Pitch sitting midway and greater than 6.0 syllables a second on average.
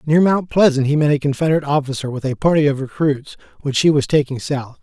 Yes: medium, 145 Hz; 6.4 syllables/s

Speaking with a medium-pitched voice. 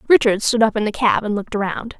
No: high, 215 Hz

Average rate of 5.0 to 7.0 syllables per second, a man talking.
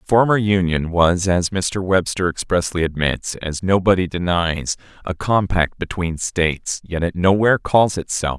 No: 4.5 syllables/s; male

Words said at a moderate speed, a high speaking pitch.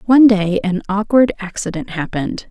Yes: average, 145 wpm; high, 205 Hz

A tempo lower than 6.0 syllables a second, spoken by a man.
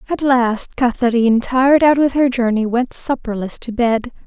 No: 4.8 syllables/s; female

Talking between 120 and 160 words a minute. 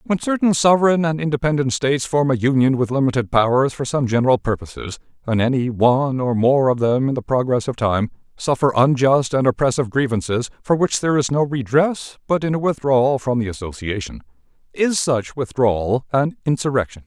No: average, 180 wpm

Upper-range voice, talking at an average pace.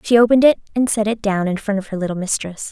No: high, 210 Hz; fast, 285 wpm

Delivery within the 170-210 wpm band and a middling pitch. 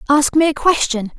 No: average, 200 wpm; very high, 285 Hz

